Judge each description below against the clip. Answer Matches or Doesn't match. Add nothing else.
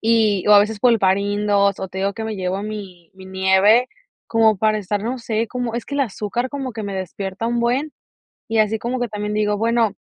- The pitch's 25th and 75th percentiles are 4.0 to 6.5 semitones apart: Doesn't match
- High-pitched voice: Matches